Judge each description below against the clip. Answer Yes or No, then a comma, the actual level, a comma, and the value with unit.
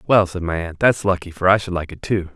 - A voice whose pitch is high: No, very low, 90 Hz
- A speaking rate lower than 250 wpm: No, fast, 305 wpm